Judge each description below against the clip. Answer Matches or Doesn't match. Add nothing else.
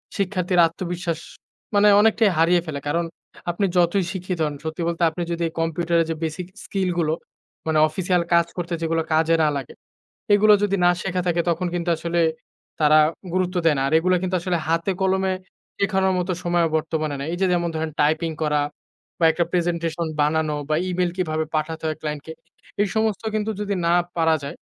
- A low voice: Doesn't match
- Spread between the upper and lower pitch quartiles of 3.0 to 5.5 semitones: Doesn't match